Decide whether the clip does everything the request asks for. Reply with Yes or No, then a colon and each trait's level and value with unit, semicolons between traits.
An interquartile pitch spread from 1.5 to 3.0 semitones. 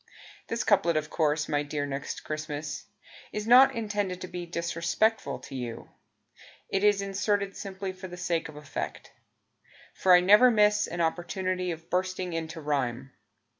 No: average, 4.3 semitones